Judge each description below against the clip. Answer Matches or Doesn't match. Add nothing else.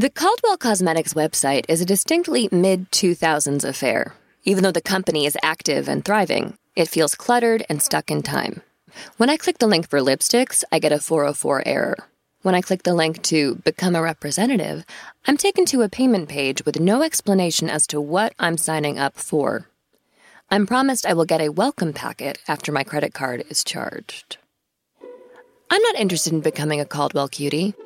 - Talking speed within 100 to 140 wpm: Doesn't match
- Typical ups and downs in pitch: Doesn't match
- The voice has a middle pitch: Matches